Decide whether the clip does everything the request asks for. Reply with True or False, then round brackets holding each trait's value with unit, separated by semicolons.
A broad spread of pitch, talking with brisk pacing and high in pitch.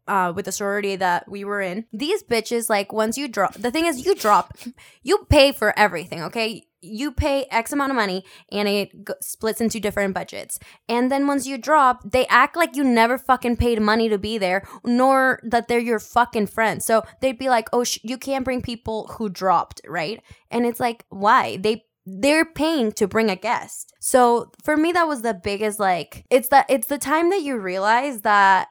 False (4.2 semitones; 210 wpm; 230 Hz)